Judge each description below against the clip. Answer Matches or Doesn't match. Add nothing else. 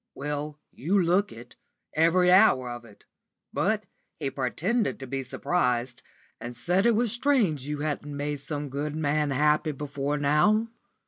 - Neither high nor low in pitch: Matches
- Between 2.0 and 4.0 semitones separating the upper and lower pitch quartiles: Doesn't match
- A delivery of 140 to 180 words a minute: Matches